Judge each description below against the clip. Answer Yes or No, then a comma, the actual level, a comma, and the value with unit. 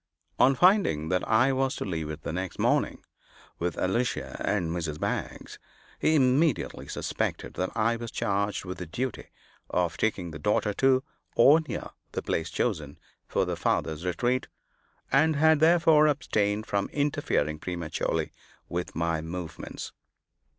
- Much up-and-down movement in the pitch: Yes, wide, 7.8 semitones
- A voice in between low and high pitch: No, low, 100 Hz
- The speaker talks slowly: No, average, 145 wpm